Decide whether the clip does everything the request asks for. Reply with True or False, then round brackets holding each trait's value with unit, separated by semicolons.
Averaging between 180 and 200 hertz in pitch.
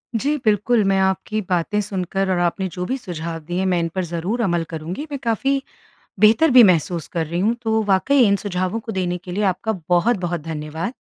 True (190 Hz)